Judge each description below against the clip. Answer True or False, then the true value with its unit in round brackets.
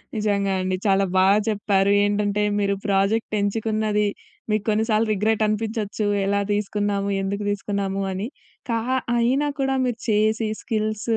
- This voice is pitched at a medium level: False (210 Hz)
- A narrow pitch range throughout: True (1.6 semitones)